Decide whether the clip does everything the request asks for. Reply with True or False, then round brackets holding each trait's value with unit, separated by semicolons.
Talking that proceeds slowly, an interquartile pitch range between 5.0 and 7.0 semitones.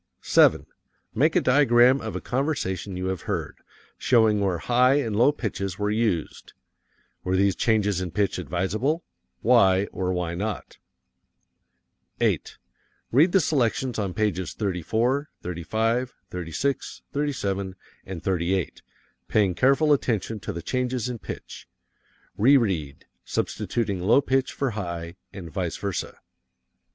True (125 wpm; 5.4 semitones)